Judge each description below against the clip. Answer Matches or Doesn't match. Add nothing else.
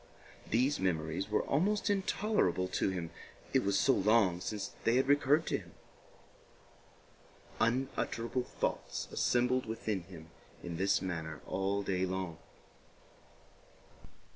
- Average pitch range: Doesn't match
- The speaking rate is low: Matches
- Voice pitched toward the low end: Matches